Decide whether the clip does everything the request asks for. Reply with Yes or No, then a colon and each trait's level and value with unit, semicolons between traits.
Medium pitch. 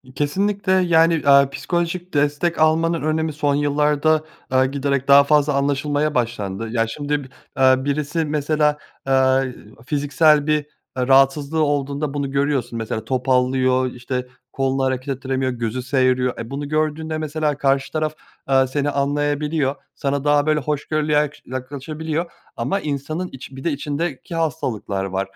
Yes: medium, 145 Hz